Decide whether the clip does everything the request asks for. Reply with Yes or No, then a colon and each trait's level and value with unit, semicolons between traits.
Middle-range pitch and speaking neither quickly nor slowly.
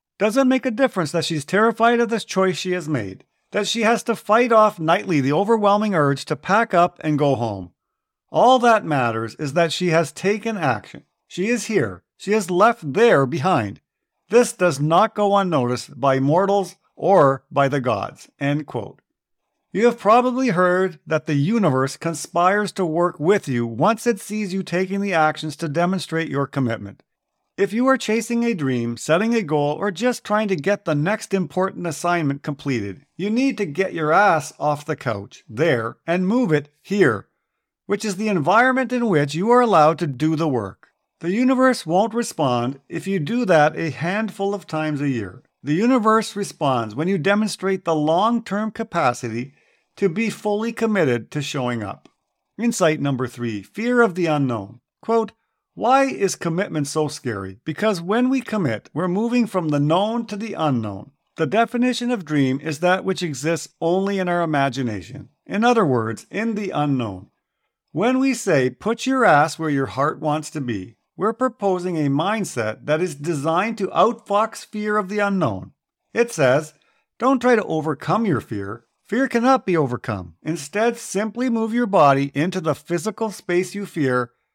Yes: medium, 175 Hz; average, 175 wpm